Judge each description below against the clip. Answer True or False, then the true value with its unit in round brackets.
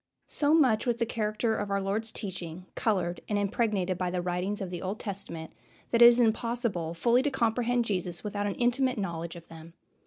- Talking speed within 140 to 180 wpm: False (195 wpm)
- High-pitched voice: True (205 Hz)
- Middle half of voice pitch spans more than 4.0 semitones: True (4.6 semitones)